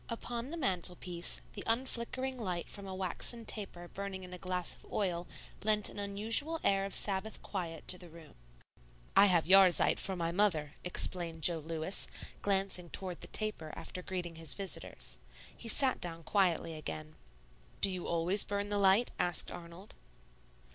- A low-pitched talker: No, medium, 185 Hz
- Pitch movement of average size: Yes, average, 3.1 semitones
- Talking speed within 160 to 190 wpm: Yes, average, 165 wpm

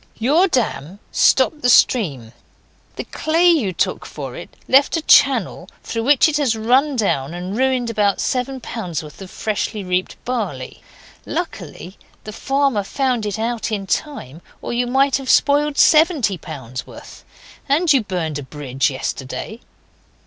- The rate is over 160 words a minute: No, average, 155 wpm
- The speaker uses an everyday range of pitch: No, wide, 7.1 semitones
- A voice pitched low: No, high, 230 Hz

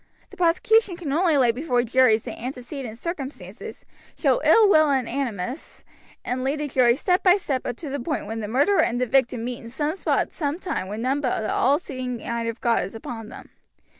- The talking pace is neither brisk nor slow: No, fast, 220 wpm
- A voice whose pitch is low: No, very high, 260 Hz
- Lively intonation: No, average, 4.4 semitones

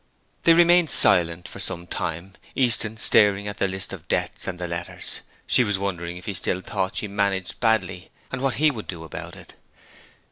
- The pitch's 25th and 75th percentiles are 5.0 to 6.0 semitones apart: No, average, 4.0 semitones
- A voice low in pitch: Yes, very low, 95 Hz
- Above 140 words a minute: Yes, average, 190 wpm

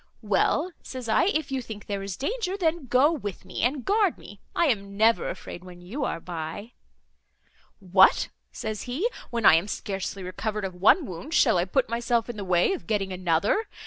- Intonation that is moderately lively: No, wide, 6.2 semitones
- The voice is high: Yes, high, 220 Hz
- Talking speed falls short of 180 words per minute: No, average, 195 wpm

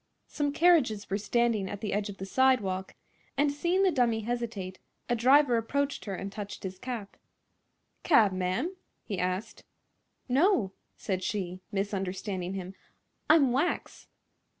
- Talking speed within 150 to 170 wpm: No, average, 140 wpm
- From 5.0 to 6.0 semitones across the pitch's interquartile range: Yes, wide, 5.6 semitones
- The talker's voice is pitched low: No, high, 215 Hz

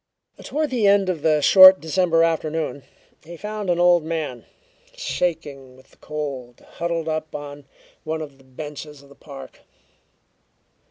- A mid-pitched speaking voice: Yes, medium, 155 Hz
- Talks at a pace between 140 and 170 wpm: Yes, average, 150 wpm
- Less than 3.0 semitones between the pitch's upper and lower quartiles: No, average, 3.6 semitones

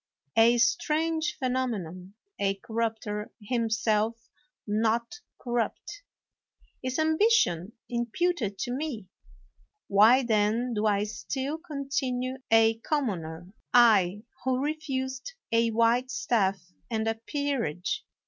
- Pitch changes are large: No, average, 3.8 semitones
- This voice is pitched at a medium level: No, high, 235 Hz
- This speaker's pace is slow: Yes, slow, 100 wpm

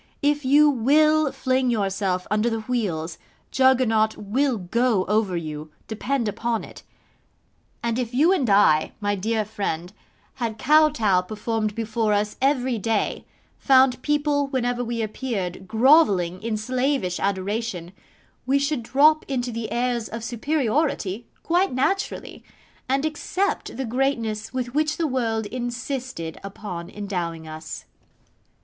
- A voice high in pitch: Yes, high, 230 Hz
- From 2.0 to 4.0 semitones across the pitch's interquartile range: No, average, 4.5 semitones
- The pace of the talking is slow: Yes, slow, 130 wpm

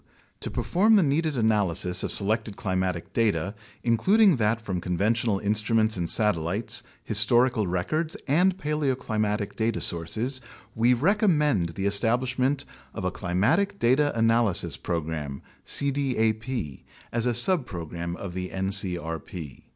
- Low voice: Yes, low, 110 Hz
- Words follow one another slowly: Yes, slow, 120 wpm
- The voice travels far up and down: Yes, wide, 6.0 semitones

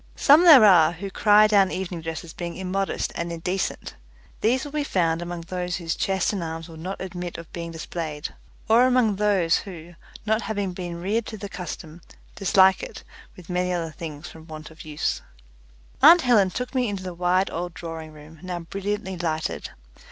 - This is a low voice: No, medium, 180 Hz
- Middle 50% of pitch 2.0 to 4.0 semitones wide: Yes, average, 3.4 semitones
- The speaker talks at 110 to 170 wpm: No, average, 190 wpm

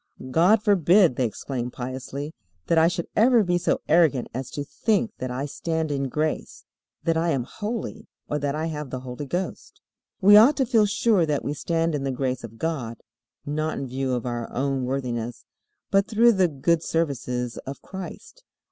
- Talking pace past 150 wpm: Yes, average, 185 wpm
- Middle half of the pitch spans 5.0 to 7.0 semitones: Yes, wide, 5.6 semitones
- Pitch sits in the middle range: Yes, medium, 150 Hz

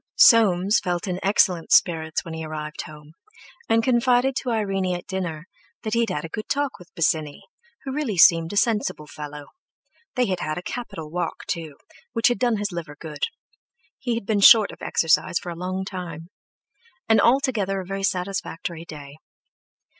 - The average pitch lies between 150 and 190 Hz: Yes, medium, 185 Hz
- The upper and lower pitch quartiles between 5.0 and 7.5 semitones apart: Yes, wide, 5.6 semitones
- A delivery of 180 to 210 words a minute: No, average, 170 wpm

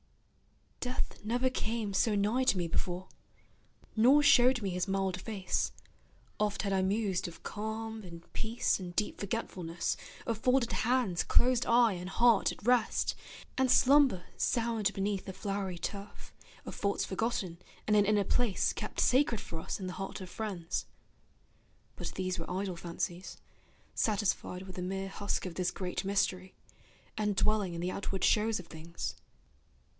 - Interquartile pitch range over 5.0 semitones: No, average, 3.4 semitones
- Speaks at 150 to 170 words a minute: Yes, average, 160 wpm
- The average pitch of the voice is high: Yes, high, 200 Hz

